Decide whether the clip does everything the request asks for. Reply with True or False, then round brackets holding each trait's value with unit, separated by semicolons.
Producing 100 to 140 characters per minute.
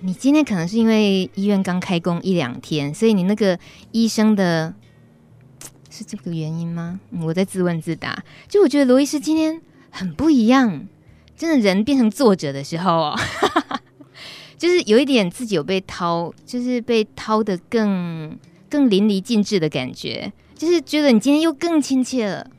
False (255 characters per minute)